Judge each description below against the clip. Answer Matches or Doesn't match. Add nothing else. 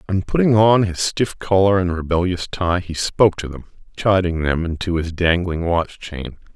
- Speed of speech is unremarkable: Matches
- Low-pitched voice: Matches